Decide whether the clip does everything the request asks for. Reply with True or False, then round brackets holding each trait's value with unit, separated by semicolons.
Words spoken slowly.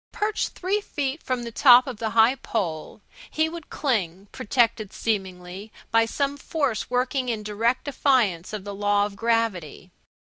False (155 wpm)